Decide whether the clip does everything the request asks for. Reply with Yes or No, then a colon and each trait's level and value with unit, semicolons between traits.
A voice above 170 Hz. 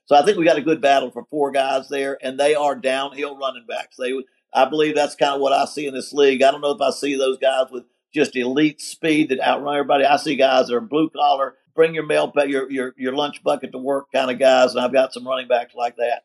No: low, 135 Hz